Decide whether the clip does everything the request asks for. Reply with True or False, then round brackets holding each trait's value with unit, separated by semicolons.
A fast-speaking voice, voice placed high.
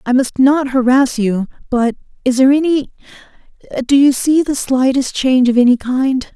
False (160 wpm; 260 Hz)